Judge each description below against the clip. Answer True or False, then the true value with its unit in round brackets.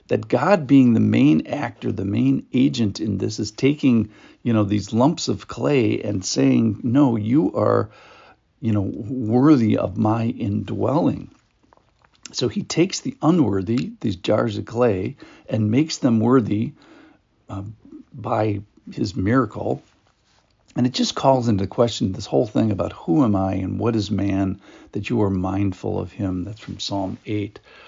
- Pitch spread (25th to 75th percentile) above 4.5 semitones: False (3.5 semitones)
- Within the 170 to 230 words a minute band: False (160 wpm)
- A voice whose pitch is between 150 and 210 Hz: False (110 Hz)